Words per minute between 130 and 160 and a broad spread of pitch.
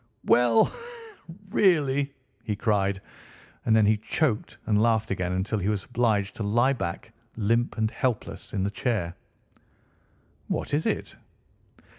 No: slow, 135 wpm; average, 3.0 semitones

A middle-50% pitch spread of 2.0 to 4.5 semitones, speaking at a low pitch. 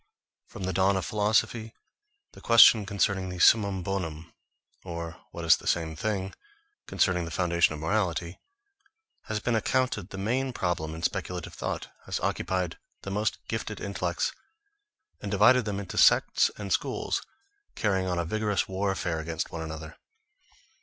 Yes: average, 3.7 semitones; very low, 95 Hz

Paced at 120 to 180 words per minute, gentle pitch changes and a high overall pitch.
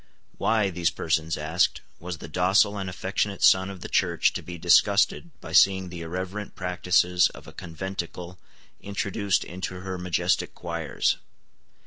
No: average, 145 wpm; narrow, 1.9 semitones; very low, 90 Hz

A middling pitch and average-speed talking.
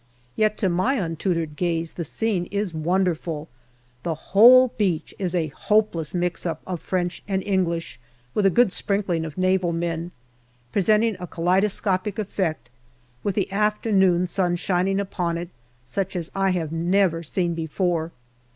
Yes: medium, 180 Hz; average, 150 wpm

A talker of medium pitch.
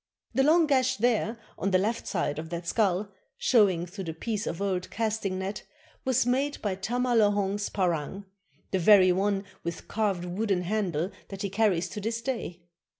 No: high, 200 Hz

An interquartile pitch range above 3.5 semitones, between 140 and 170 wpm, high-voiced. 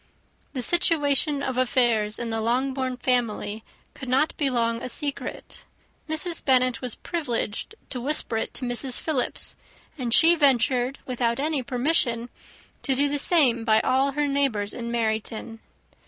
No: average, 3.2 semitones; average, 150 wpm; very high, 255 Hz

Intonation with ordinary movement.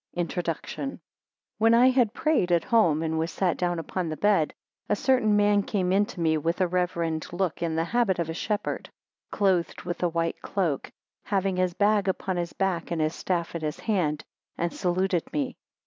Yes: average, 3.5 semitones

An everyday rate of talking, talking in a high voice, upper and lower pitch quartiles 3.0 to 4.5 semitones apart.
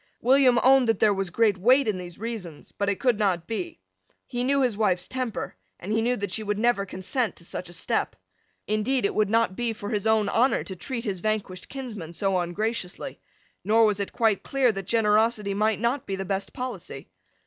No: fast, 210 wpm; high, 215 Hz; average, 3.5 semitones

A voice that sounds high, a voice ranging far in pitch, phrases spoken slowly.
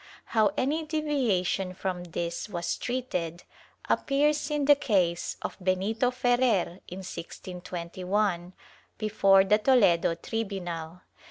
Yes: high, 195 Hz; wide, 5.9 semitones; slow, 110 wpm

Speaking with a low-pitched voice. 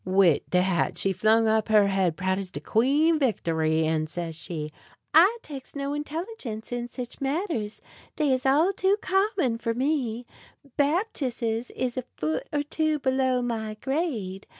No: high, 245 Hz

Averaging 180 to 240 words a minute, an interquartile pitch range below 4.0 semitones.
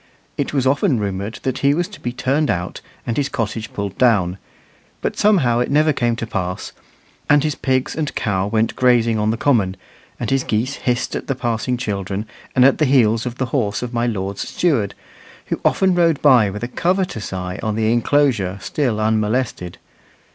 No: average, 190 wpm; average, 4.5 semitones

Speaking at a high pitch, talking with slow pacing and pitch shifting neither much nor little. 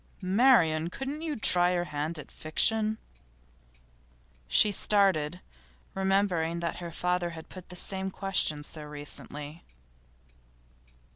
No: medium, 180 Hz; slow, 115 wpm; average, 3.8 semitones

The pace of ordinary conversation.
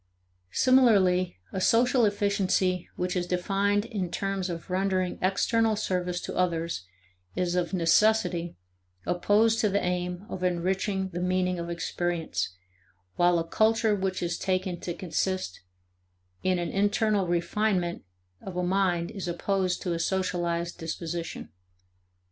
No: slow, 130 wpm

